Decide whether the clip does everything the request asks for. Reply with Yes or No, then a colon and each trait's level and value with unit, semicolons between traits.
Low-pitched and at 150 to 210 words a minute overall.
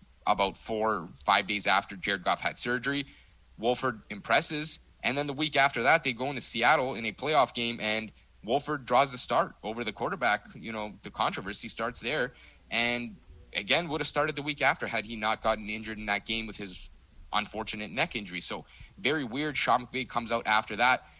Yes: low, 115 Hz; average, 200 wpm